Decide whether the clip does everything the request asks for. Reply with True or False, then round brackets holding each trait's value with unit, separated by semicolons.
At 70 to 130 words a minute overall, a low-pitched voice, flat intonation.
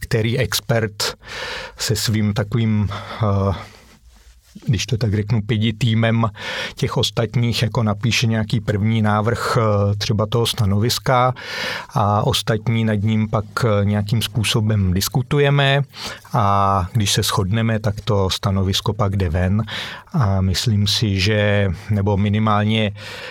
True (115 wpm; 110 Hz; 2.3 semitones)